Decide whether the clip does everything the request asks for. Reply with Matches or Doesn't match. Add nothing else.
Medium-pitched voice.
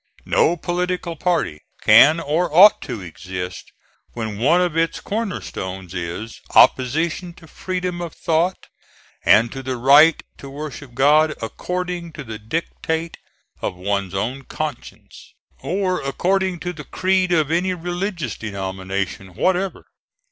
Matches